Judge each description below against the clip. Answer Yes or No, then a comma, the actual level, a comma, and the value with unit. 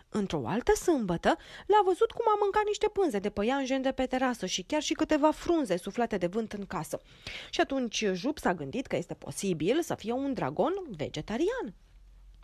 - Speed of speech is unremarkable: No, fast, 185 wpm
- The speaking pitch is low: No, very high, 255 Hz